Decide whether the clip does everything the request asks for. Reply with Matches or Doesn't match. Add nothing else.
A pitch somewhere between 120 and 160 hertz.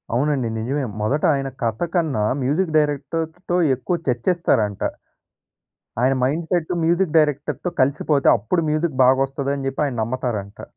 Matches